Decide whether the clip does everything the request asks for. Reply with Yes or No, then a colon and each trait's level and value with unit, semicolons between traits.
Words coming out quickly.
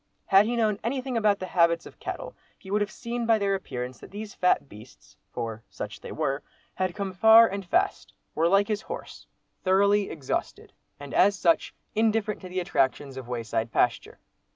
No: average, 185 wpm